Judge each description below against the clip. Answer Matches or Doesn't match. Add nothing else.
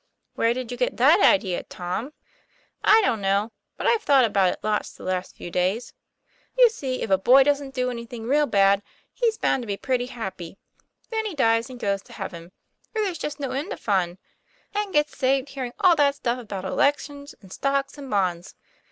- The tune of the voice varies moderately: Doesn't match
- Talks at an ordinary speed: Doesn't match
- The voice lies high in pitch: Matches